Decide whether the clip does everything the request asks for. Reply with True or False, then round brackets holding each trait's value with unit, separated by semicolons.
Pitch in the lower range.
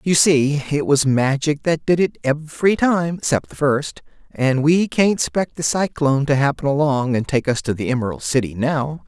False (145 Hz)